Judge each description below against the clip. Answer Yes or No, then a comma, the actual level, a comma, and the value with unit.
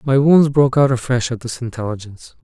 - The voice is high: No, low, 125 Hz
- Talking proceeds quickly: No, average, 195 wpm